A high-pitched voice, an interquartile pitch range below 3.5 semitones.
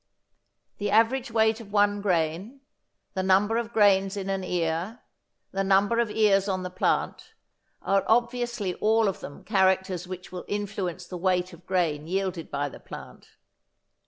Yes: high, 195 Hz; average, 2.8 semitones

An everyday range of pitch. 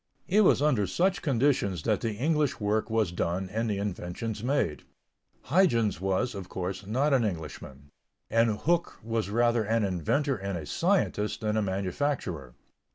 No: wide, 5.8 semitones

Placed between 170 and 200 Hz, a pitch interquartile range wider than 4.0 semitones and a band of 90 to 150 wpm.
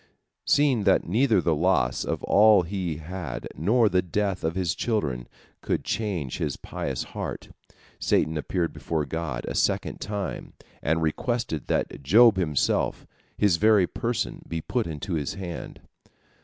No: very low, 90 Hz; average, 4.9 semitones; average, 145 wpm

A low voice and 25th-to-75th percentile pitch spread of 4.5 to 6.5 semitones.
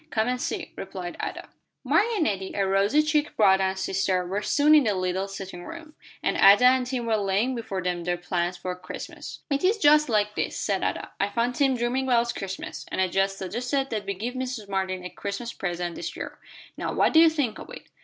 No: high, 205 Hz; average, 5.1 semitones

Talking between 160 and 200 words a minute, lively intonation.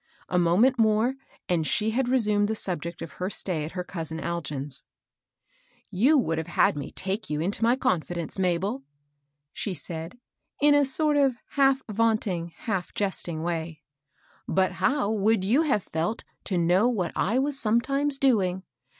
Yes: average, 170 wpm; wide, 6.1 semitones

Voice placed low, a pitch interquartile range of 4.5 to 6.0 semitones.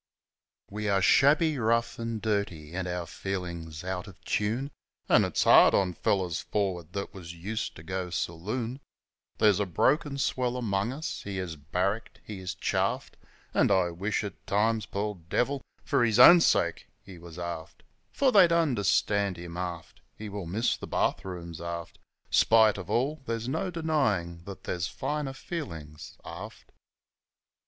Yes: low, 100 Hz; average, 5.0 semitones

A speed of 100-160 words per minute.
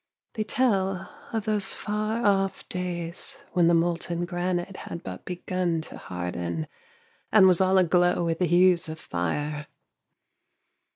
Yes: slow, 135 wpm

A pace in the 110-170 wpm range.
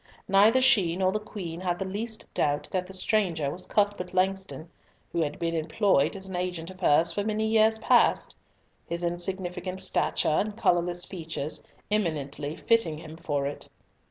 Yes: average, 165 wpm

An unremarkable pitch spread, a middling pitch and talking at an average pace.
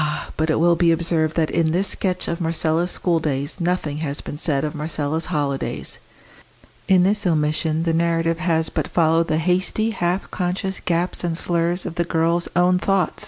No: narrow, 2.0 semitones; medium, 165 Hz; average, 175 wpm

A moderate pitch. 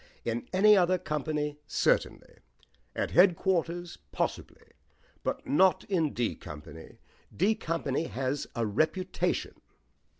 Yes: medium, 165 Hz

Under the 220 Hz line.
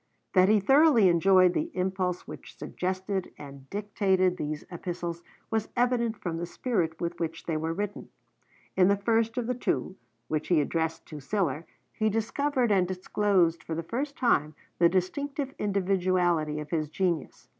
Yes: medium, 185 Hz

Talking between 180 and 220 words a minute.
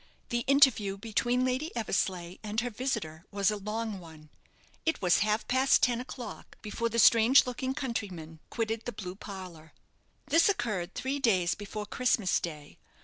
No: average, 155 wpm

